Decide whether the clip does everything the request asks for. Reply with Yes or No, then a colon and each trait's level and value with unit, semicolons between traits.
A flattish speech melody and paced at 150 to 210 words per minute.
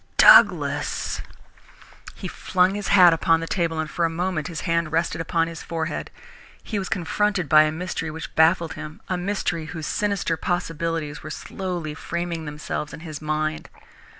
Yes: narrow, 2.2 semitones; average, 165 wpm